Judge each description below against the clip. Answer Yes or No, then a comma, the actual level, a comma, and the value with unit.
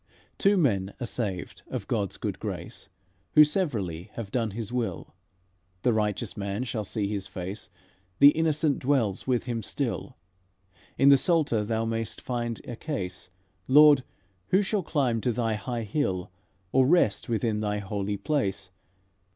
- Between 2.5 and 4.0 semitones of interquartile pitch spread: No, average, 5.3 semitones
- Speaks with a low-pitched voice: Yes, low, 115 Hz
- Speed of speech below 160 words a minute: Yes, average, 150 wpm